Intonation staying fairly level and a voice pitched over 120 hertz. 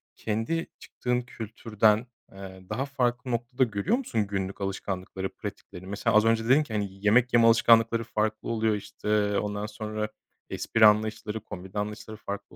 No: narrow, 2.1 semitones; low, 110 Hz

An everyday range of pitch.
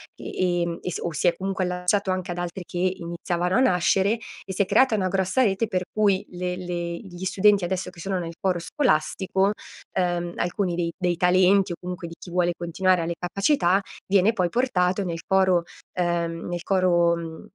No: narrow, 1.8 semitones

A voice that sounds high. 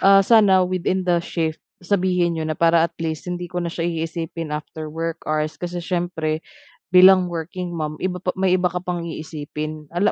No: medium, 170 Hz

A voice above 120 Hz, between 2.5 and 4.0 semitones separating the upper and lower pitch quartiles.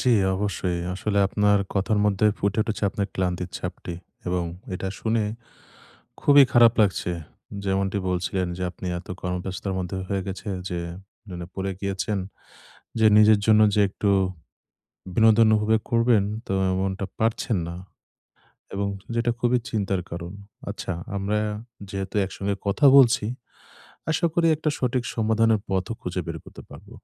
No: low, 100 Hz; average, 2.9 semitones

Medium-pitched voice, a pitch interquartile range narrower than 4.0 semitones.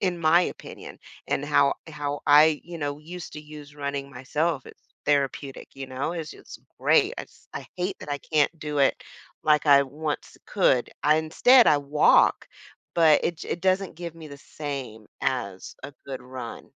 Yes: medium, 150 Hz; average, 2.9 semitones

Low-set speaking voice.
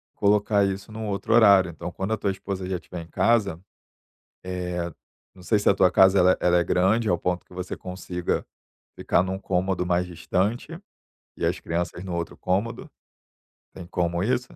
Yes: very low, 95 Hz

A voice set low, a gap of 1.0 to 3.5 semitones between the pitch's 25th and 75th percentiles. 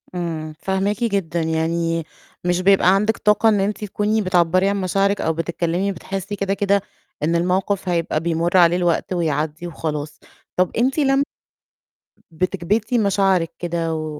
No: medium, 180 Hz; average, 3.2 semitones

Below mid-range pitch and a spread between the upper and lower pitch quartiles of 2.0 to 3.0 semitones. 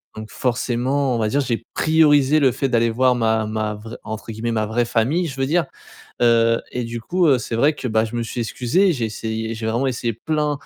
No: low, 120 Hz; average, 3.5 semitones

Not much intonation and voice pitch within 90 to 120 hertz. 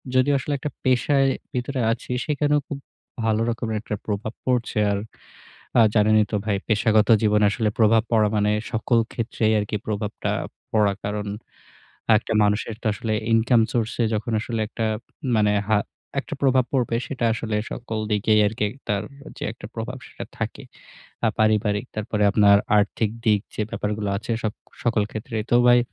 Yes: narrow, 2.0 semitones; low, 110 Hz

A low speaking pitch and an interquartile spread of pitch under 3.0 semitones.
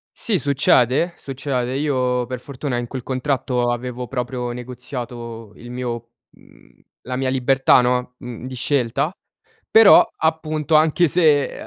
Yes: low, 125 Hz; narrow, 2.6 semitones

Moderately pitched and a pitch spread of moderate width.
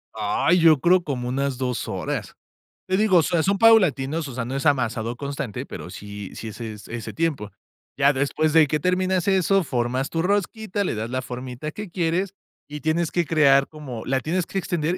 No: medium, 150 Hz; wide, 5.7 semitones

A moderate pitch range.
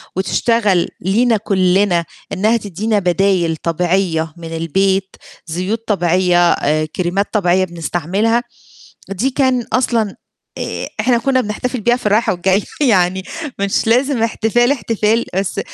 Yes: average, 4.3 semitones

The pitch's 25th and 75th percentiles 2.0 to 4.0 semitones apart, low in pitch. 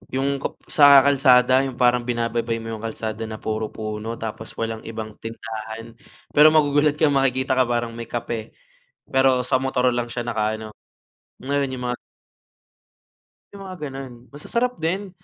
Yes: average, 3.5 semitones; low, 125 Hz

